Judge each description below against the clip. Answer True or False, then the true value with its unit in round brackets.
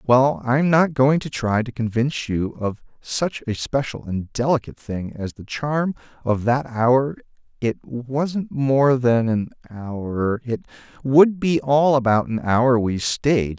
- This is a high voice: False (125 Hz)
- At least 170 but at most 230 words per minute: False (155 wpm)